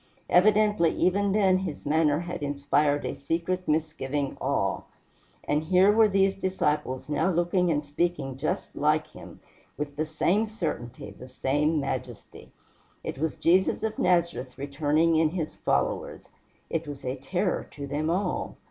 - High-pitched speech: No, medium, 160 Hz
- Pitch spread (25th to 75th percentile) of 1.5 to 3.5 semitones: No, average, 4.1 semitones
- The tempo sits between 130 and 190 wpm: Yes, average, 150 wpm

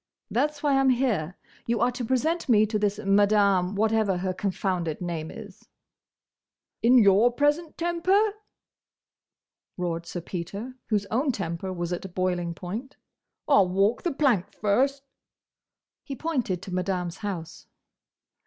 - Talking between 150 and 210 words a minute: No, slow, 135 wpm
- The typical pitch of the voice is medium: No, high, 205 Hz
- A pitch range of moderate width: No, wide, 5.9 semitones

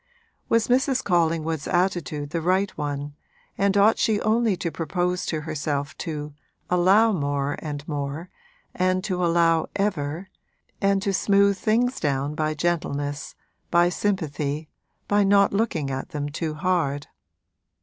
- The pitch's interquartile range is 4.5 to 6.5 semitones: Yes, average, 5.0 semitones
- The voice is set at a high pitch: No, medium, 170 Hz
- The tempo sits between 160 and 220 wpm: No, slow, 135 wpm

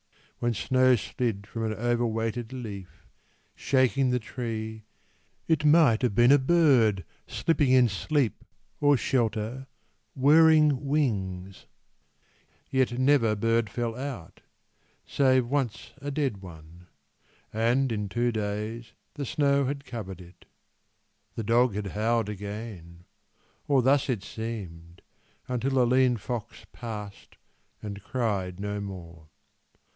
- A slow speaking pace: Yes, slow, 120 wpm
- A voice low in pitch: Yes, low, 115 Hz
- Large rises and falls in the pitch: No, average, 4.2 semitones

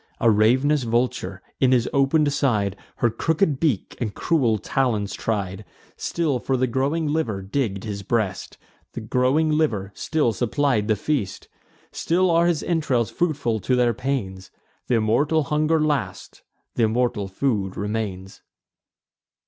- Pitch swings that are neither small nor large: No, wide, 5.7 semitones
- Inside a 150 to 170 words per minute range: No, average, 140 wpm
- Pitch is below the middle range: Yes, low, 125 Hz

